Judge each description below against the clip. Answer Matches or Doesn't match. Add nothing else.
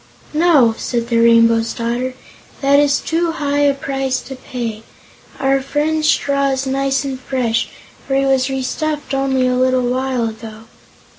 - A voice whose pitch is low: Doesn't match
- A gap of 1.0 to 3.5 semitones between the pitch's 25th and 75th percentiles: Matches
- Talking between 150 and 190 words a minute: Matches